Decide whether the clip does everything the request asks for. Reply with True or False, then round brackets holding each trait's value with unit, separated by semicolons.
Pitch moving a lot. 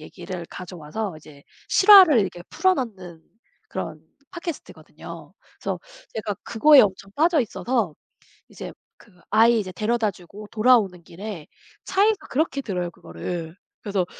True (6.1 semitones)